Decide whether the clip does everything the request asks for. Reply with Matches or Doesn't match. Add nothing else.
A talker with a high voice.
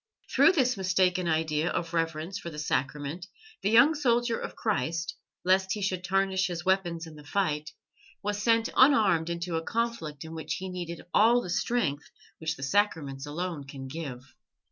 Doesn't match